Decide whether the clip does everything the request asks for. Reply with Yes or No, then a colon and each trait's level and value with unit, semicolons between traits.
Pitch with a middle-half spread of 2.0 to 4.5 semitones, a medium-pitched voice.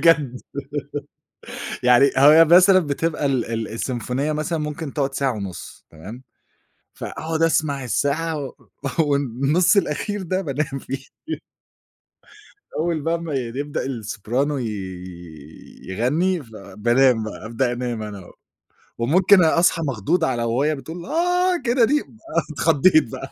No: average, 5.1 semitones; medium, 145 Hz